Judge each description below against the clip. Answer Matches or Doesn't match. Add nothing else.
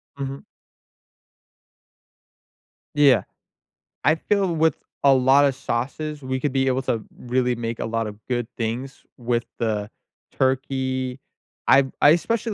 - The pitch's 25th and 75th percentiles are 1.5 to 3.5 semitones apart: Matches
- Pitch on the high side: Doesn't match